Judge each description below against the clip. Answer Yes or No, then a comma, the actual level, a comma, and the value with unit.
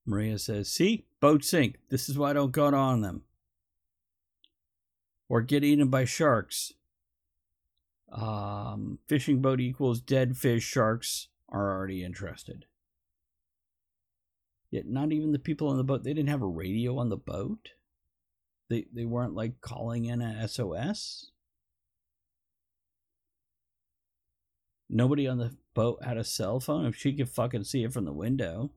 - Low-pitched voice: Yes, low, 110 Hz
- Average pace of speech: Yes, average, 145 wpm